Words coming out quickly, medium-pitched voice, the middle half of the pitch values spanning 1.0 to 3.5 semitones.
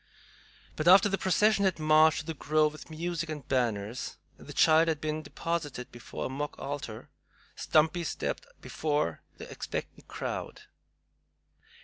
No: average, 145 wpm; medium, 155 Hz; narrow, 2.6 semitones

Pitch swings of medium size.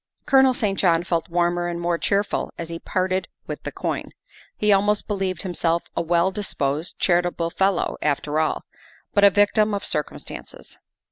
Yes: average, 3.0 semitones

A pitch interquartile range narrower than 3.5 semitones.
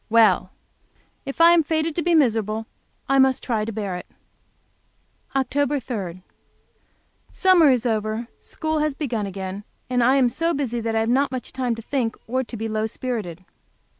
No: average, 4.3 semitones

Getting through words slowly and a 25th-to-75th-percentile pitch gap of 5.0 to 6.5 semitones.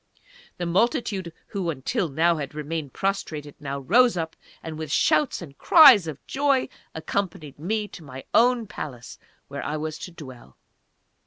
No: average, 155 wpm; wide, 5.4 semitones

